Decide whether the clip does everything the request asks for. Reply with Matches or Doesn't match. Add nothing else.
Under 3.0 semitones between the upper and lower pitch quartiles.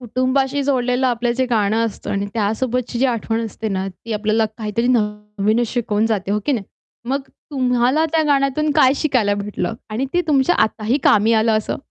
Doesn't match